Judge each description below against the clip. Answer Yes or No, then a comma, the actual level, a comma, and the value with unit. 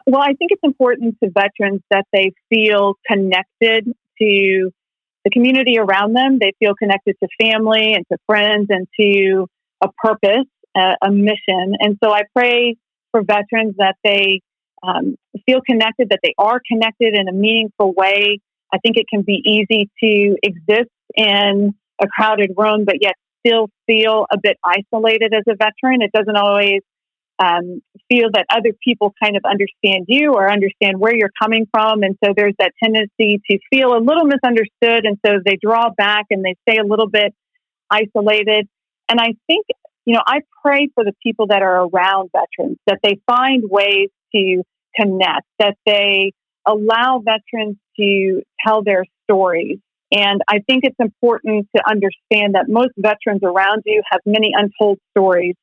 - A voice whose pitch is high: Yes, high, 210 Hz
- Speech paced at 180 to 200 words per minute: No, average, 165 wpm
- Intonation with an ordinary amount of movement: No, narrow, 2.3 semitones